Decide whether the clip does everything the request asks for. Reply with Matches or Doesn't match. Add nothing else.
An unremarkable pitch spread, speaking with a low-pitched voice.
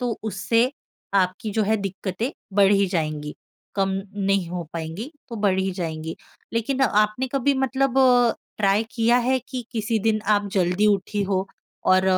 Doesn't match